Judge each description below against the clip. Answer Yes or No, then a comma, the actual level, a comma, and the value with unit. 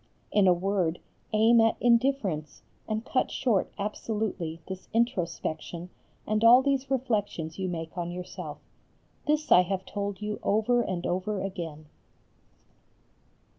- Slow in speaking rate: Yes, slow, 130 wpm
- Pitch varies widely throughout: No, average, 4.5 semitones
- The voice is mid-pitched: No, high, 200 Hz